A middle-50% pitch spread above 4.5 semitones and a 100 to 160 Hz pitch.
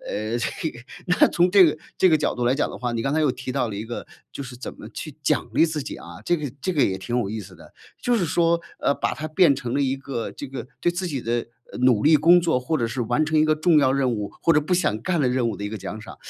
Yes: average, 5.0 semitones; low, 135 Hz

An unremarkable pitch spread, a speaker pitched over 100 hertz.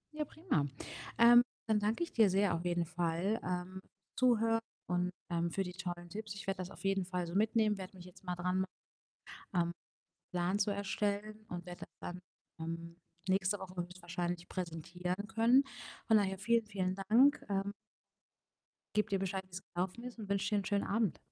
Yes: average, 3.0 semitones; high, 190 Hz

